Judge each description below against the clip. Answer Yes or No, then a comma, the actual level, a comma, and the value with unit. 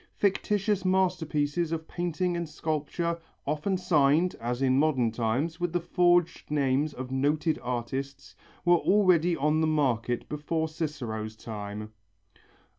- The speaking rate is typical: No, slow, 125 wpm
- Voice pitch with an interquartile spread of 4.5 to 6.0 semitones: Yes, average, 4.8 semitones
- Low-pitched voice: No, medium, 155 Hz